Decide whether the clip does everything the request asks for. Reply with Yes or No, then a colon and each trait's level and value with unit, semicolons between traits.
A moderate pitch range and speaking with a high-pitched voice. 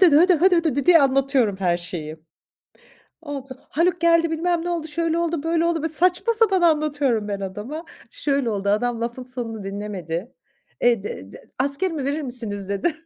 No: wide, 7.9 semitones; very high, 280 Hz